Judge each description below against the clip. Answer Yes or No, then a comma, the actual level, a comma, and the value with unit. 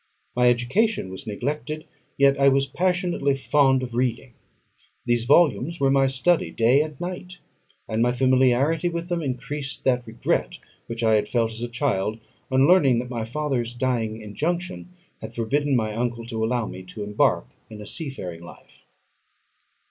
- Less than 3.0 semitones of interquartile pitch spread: No, average, 4.1 semitones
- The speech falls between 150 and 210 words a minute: Yes, average, 165 wpm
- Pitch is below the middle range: Yes, low, 130 Hz